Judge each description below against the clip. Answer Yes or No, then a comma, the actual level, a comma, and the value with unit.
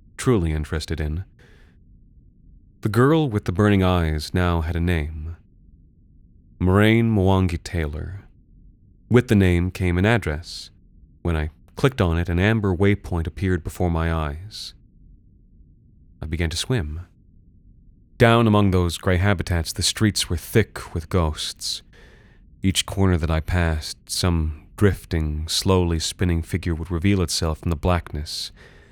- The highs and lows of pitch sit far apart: No, average, 3.4 semitones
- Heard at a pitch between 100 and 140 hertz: No, very low, 90 Hz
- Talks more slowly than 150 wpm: Yes, slow, 135 wpm